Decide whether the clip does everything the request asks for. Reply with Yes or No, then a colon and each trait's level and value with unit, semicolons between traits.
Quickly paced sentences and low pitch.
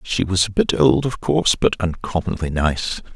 No: average, 190 wpm; very low, 95 Hz